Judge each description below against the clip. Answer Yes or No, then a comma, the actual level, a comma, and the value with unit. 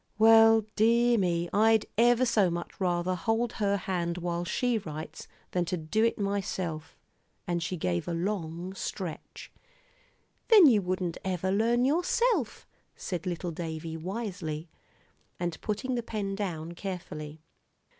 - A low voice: No, medium, 185 Hz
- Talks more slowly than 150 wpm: Yes, slow, 135 wpm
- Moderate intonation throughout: Yes, average, 4.6 semitones